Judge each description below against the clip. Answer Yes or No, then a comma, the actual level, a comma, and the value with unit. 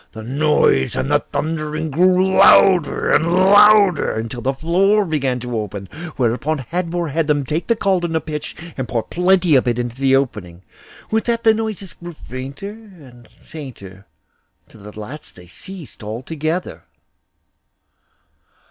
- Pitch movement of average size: No, wide, 6.7 semitones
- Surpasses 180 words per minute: No, average, 145 wpm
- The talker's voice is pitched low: No, medium, 155 Hz